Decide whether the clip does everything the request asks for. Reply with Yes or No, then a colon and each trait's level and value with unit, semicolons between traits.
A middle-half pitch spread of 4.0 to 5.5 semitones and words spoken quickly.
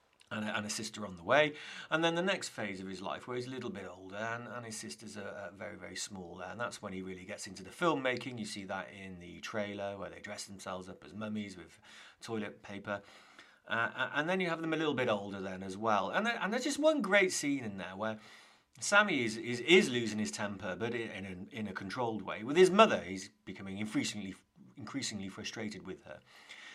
Yes: average, 4.4 semitones; fast, 235 wpm